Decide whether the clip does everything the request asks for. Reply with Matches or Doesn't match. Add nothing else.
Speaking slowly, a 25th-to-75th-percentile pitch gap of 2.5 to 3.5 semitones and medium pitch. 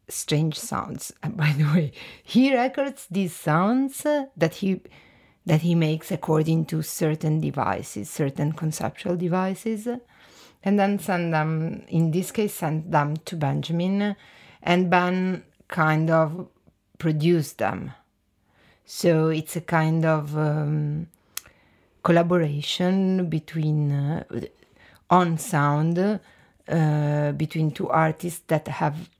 Matches